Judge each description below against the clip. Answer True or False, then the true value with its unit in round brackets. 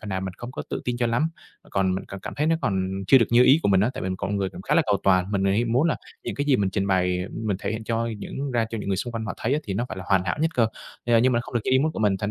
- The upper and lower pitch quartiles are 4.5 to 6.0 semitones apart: False (4.0 semitones)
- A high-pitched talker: False (110 Hz)